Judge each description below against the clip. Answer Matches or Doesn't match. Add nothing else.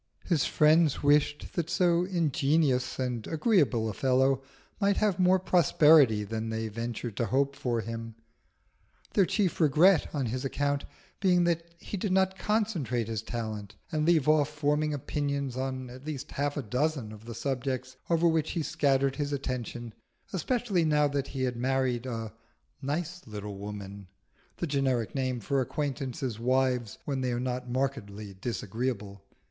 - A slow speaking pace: Doesn't match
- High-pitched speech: Doesn't match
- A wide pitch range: Doesn't match